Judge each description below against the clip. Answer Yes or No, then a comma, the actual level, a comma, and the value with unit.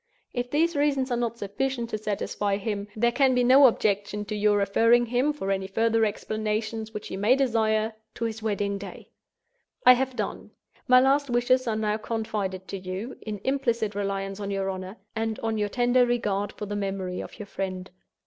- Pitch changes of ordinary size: Yes, average, 3.2 semitones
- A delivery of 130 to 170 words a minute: No, average, 190 wpm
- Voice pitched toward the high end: Yes, high, 220 Hz